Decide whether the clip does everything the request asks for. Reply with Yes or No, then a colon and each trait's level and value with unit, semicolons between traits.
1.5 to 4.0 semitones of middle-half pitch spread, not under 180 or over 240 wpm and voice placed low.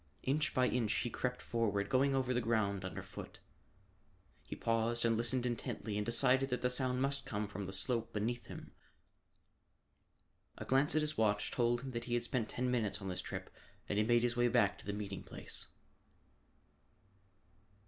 Yes: average, 3.1 semitones; average, 185 wpm; low, 120 Hz